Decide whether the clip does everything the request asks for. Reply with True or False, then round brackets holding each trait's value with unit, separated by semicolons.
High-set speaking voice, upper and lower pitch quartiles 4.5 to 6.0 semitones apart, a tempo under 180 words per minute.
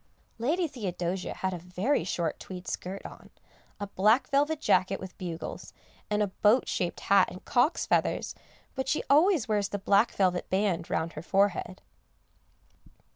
True (195 Hz; 5.0 semitones; 155 wpm)